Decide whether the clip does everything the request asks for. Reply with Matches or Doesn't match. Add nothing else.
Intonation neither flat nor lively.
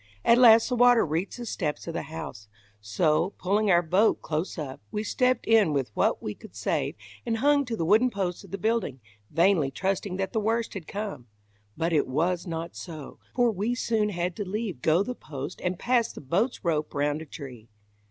Doesn't match